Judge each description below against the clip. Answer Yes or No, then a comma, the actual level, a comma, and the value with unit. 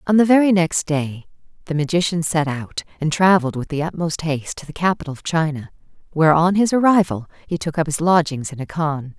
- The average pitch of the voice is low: No, medium, 160 Hz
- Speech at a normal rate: No, fast, 210 wpm